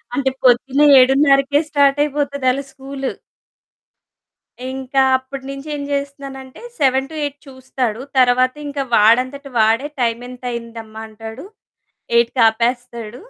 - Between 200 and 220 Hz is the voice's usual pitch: No, very high, 260 Hz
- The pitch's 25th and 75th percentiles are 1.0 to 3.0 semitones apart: Yes, narrow, 2.5 semitones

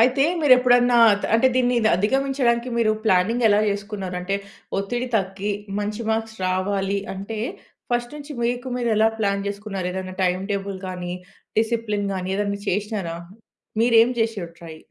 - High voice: Yes, high, 210 Hz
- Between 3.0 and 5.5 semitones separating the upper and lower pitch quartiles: Yes, average, 3.6 semitones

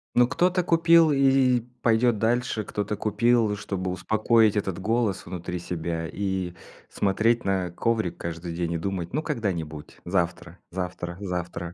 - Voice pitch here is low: Yes, low, 100 Hz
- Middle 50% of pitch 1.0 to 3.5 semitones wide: No, average, 5.0 semitones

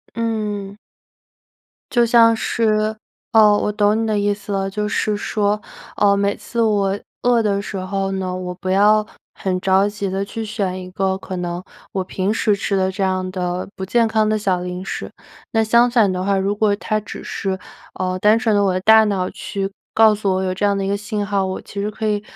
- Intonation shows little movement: Yes, narrow, 2.1 semitones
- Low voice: No, high, 200 Hz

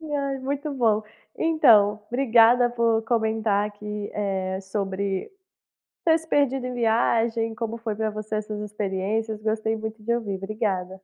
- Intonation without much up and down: Yes, narrow, 2.3 semitones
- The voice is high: Yes, high, 220 Hz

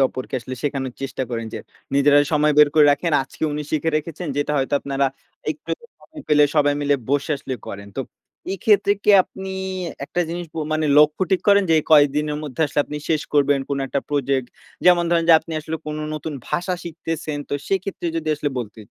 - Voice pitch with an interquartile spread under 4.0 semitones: Yes, average, 2.7 semitones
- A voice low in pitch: No, medium, 150 Hz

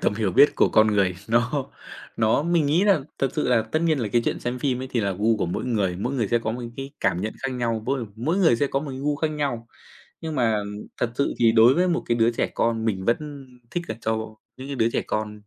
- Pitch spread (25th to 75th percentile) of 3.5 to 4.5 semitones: Yes, average, 4.1 semitones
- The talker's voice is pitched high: No, low, 120 Hz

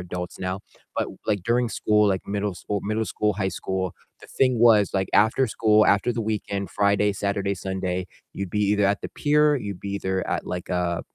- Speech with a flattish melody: Yes, narrow, 2.2 semitones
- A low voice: Yes, low, 100 Hz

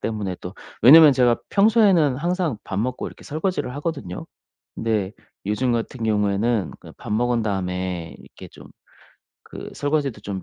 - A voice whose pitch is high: No, low, 120 Hz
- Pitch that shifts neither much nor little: No, wide, 6.5 semitones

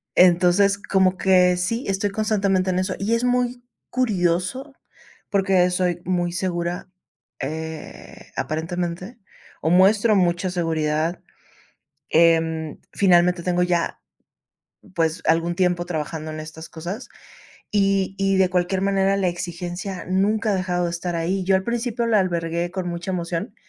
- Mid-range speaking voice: Yes, medium, 180 Hz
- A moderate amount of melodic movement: No, narrow, 2.3 semitones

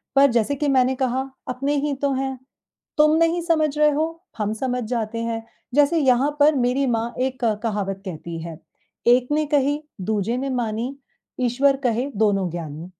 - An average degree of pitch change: Yes, average, 3.9 semitones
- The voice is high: Yes, very high, 255 Hz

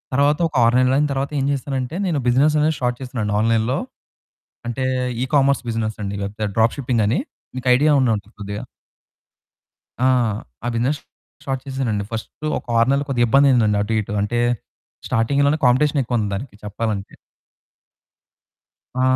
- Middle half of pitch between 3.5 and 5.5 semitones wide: Yes, average, 3.8 semitones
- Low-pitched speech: Yes, low, 125 Hz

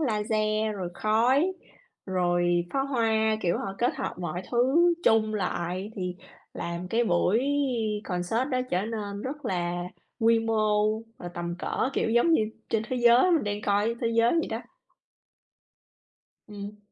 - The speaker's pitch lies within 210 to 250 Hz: Yes, high, 215 Hz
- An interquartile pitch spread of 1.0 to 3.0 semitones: No, average, 4.4 semitones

